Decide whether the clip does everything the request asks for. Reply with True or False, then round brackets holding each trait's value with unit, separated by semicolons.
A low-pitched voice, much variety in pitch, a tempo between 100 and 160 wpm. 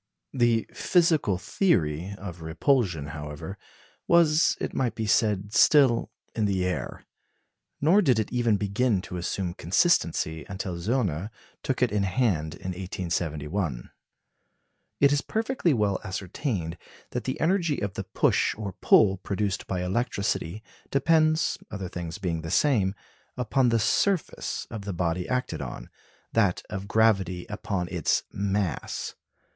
True (100 Hz; 5.7 semitones; 135 wpm)